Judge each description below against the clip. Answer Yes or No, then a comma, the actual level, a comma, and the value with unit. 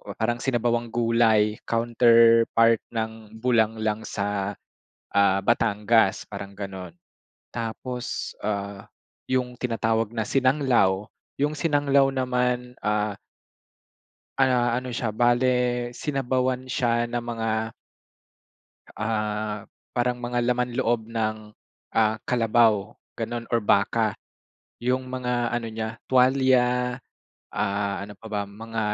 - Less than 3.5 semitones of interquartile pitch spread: Yes, narrow, 2.5 semitones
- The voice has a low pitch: Yes, low, 115 Hz